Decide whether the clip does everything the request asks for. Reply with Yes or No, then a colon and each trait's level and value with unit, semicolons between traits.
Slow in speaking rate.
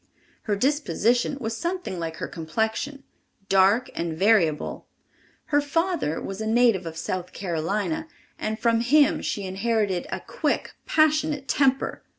Yes: slow, 130 wpm